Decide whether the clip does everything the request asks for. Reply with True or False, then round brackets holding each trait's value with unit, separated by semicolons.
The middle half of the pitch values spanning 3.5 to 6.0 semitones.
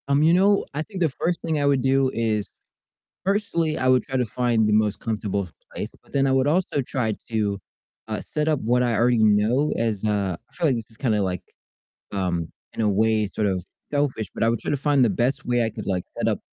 True (5.0 semitones)